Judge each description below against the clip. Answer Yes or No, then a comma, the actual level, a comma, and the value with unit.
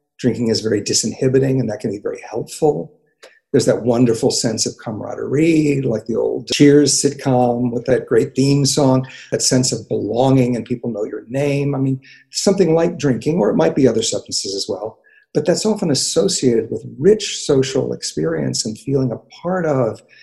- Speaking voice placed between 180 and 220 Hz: No, low, 135 Hz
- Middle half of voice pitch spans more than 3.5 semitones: Yes, average, 4.0 semitones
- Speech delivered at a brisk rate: No, average, 180 wpm